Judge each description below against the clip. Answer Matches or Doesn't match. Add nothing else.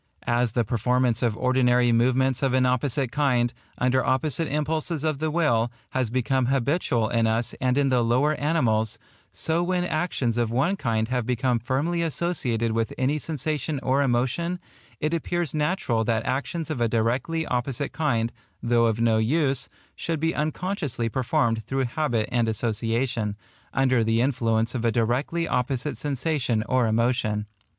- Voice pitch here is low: Matches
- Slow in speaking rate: Doesn't match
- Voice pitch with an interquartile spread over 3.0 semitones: Matches